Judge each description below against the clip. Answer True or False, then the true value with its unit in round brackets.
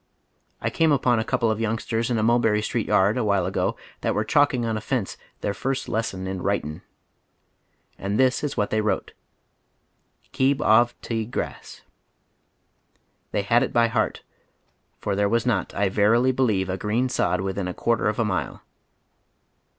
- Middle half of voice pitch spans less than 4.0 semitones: True (3.2 semitones)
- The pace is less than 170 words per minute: False (175 wpm)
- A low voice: True (110 Hz)